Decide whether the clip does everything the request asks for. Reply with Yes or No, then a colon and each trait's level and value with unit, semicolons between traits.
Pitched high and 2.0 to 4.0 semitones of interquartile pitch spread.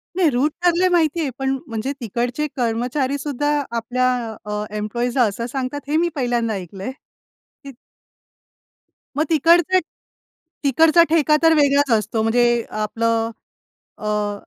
No: very high, 255 Hz; average, 4.8 semitones